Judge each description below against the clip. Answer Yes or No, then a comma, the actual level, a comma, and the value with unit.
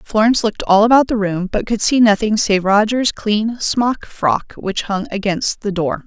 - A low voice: No, high, 210 Hz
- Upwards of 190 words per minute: Yes, average, 200 wpm